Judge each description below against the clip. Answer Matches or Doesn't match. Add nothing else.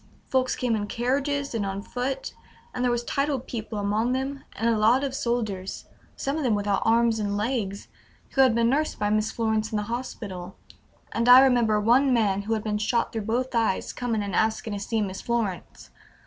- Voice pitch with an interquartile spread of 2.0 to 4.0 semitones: Matches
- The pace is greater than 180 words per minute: Matches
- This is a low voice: Doesn't match